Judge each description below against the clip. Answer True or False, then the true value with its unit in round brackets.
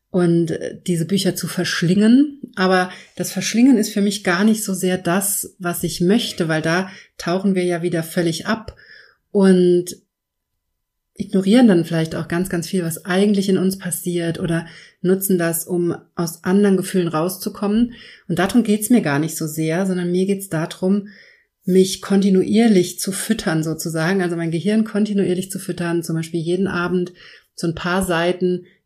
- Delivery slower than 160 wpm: False (170 wpm)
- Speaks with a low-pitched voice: False (180 Hz)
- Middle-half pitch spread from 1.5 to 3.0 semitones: True (2.5 semitones)